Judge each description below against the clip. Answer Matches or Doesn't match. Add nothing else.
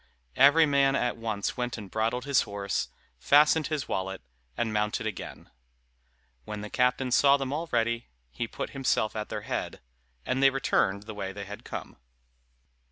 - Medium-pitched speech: Doesn't match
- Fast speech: Doesn't match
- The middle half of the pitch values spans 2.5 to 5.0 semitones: Matches